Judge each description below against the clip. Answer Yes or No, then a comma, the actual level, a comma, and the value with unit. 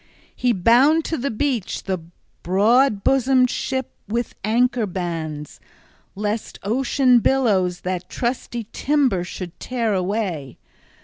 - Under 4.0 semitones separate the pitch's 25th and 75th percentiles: No, wide, 5.5 semitones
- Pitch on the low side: No, high, 225 Hz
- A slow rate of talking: Yes, slow, 115 wpm